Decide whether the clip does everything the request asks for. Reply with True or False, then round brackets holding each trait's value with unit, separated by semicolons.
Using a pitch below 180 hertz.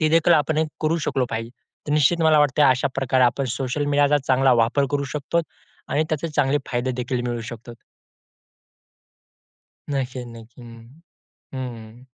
True (135 Hz)